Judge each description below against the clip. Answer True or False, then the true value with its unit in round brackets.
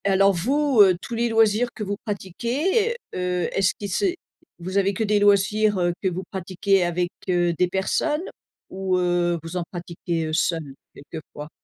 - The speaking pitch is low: False (190 Hz)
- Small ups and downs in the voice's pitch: False (3.2 semitones)